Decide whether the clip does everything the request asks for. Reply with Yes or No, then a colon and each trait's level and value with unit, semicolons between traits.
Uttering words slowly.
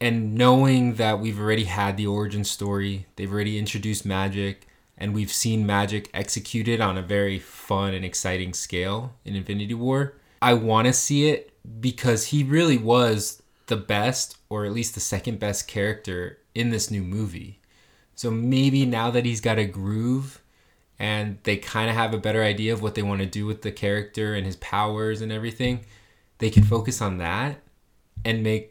No: average, 180 wpm